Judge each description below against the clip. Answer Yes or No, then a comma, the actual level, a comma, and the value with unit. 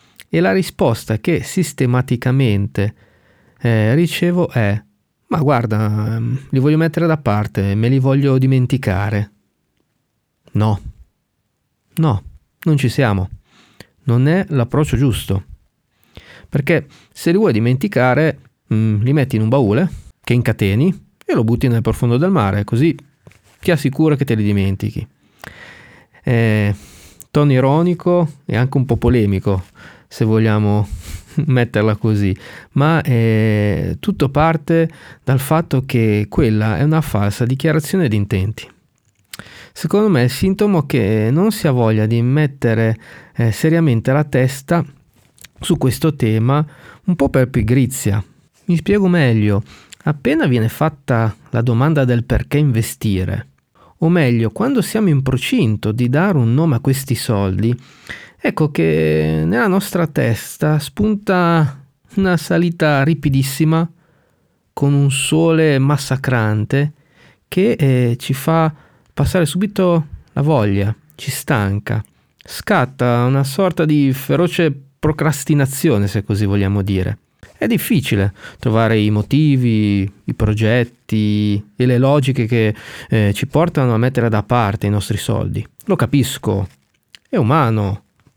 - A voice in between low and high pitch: No, low, 125 Hz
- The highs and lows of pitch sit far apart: Yes, wide, 5.8 semitones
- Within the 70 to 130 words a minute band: Yes, average, 125 wpm